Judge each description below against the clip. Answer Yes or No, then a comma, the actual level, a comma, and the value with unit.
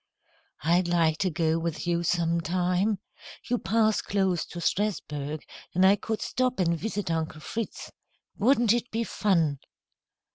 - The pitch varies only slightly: No, average, 4.3 semitones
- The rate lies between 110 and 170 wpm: Yes, average, 140 wpm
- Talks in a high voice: No, medium, 180 Hz